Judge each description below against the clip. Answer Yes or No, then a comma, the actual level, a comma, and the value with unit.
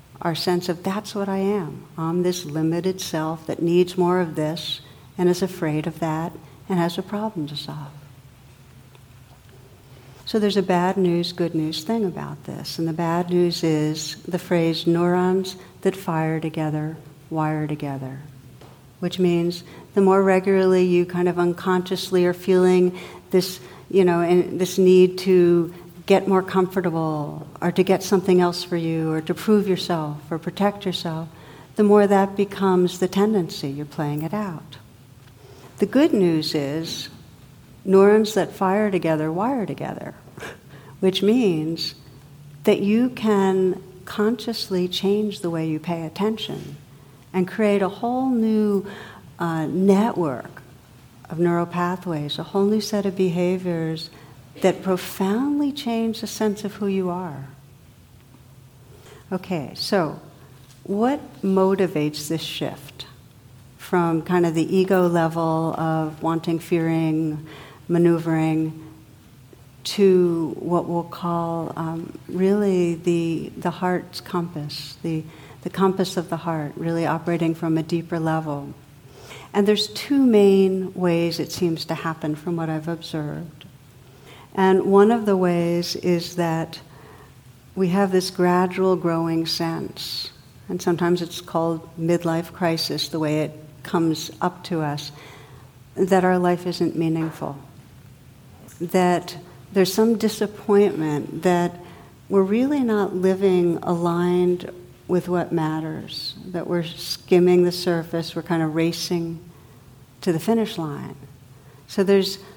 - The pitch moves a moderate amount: Yes, average, 3.4 semitones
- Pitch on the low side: No, medium, 170 Hz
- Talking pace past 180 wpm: No, slow, 135 wpm